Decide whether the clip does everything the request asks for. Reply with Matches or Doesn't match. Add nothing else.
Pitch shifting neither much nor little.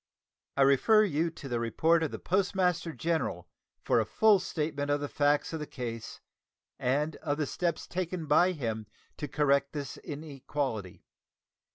Matches